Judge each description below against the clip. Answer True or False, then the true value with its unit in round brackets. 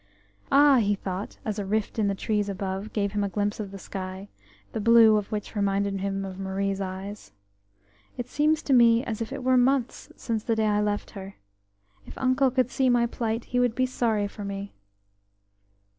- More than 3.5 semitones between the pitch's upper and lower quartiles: False (3.2 semitones)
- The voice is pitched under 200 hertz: False (210 Hz)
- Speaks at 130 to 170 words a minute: False (200 wpm)